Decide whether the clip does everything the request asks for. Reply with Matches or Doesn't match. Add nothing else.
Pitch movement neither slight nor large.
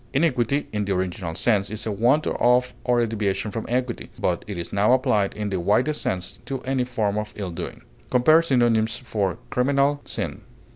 Matches